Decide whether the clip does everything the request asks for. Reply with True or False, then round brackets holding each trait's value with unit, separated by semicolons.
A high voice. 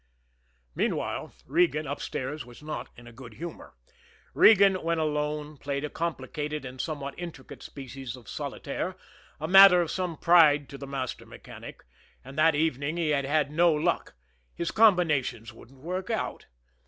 False (150 Hz)